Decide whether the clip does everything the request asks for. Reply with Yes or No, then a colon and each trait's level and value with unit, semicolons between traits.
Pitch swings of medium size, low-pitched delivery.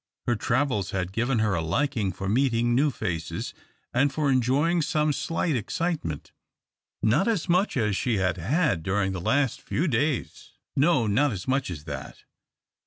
No: wide, 7.0 semitones; low, 120 Hz